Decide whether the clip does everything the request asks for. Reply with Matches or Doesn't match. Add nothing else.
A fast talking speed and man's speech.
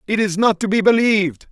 Matches